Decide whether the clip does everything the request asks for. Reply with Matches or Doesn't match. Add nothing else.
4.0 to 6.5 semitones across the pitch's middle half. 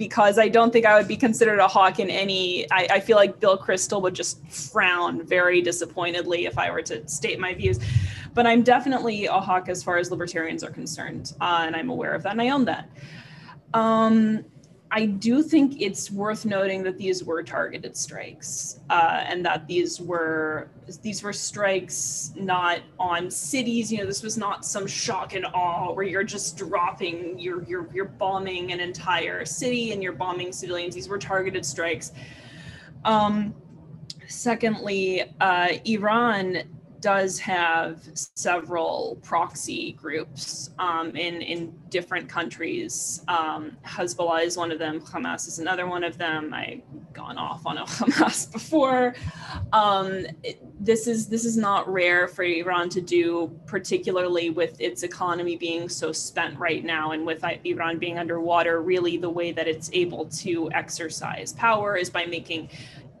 Doesn't match